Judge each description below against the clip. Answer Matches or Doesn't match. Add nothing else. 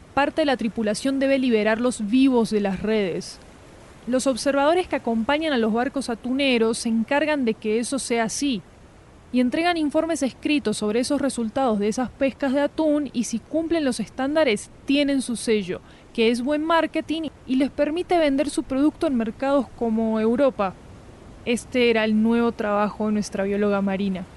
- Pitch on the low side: Doesn't match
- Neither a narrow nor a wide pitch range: Matches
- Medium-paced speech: Matches